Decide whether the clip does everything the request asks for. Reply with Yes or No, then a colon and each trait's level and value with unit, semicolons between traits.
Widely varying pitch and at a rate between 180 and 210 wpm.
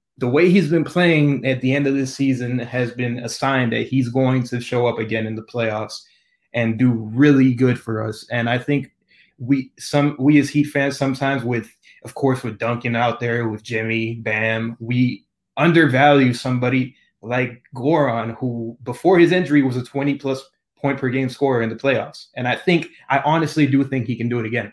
No: average, 2.9 semitones; average, 200 wpm